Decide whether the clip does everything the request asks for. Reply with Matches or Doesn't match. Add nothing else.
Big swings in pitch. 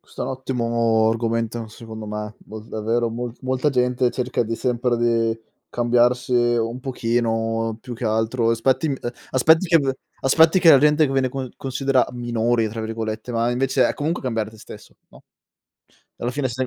Doesn't match